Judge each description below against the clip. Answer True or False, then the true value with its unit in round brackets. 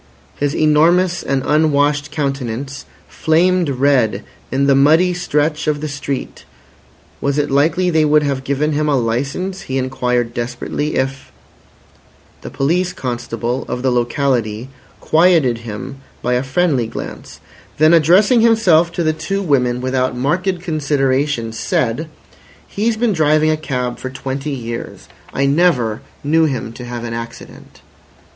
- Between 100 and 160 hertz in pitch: True (140 Hz)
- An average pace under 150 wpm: True (140 wpm)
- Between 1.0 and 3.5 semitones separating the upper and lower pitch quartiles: False (3.9 semitones)